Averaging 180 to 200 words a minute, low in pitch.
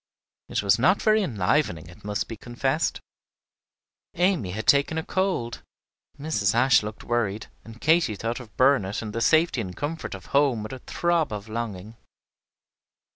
No: average, 160 wpm; low, 120 Hz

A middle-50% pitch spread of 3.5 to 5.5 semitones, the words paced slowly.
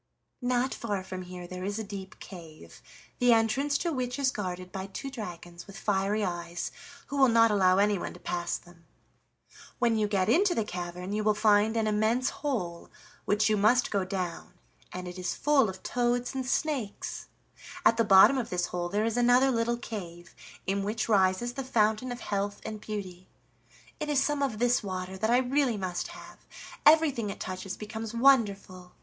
No: average, 4.7 semitones; average, 185 wpm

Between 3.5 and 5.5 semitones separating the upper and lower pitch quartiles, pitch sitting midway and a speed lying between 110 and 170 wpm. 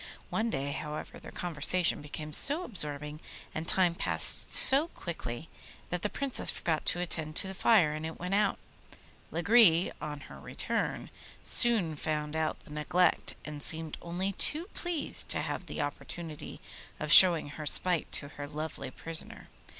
Yes: average, 3.8 semitones; medium, 165 Hz; average, 160 wpm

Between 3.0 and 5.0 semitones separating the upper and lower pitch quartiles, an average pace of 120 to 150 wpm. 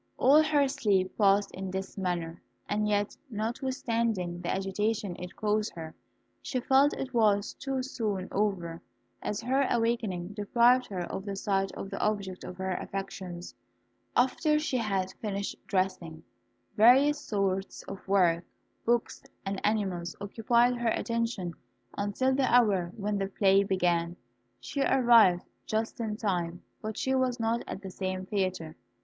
Yes: average, 3.9 semitones; average, 145 wpm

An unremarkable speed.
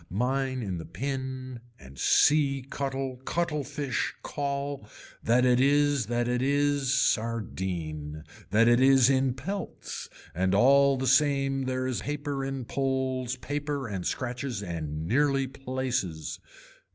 No: slow, 130 wpm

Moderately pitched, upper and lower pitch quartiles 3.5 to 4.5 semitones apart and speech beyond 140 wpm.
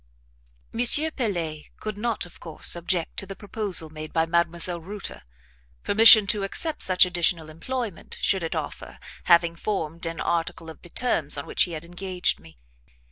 Yes: medium, 175 Hz; average, 3.9 semitones; average, 165 wpm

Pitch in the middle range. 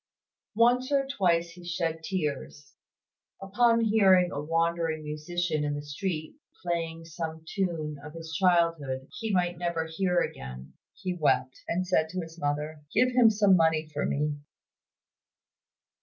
Yes: medium, 165 Hz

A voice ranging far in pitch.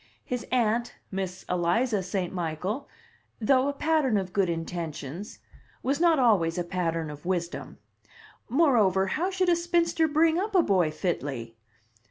Yes: wide, 8.5 semitones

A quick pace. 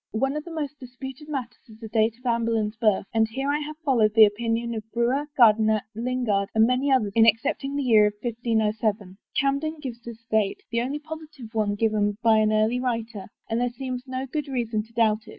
Yes: fast, 215 wpm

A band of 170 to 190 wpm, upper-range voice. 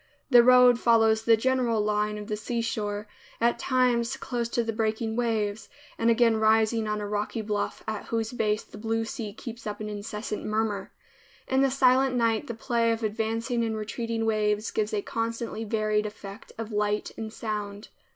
Yes: average, 180 wpm; high, 225 Hz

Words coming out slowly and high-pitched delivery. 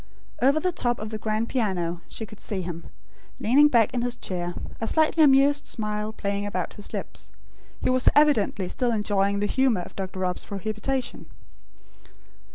No: average, 165 wpm; high, 215 Hz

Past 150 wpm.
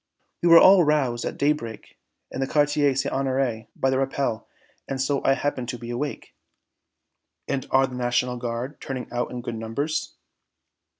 Yes: average, 170 wpm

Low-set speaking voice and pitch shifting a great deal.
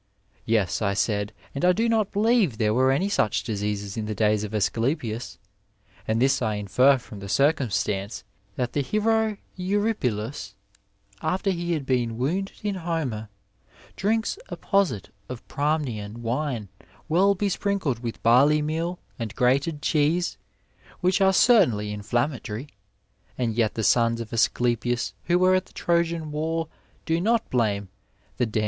Yes: low, 130 Hz; wide, 8.0 semitones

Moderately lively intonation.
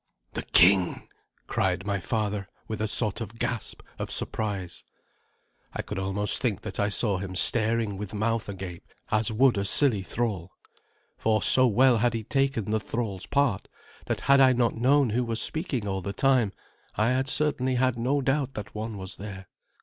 Yes: average, 4.0 semitones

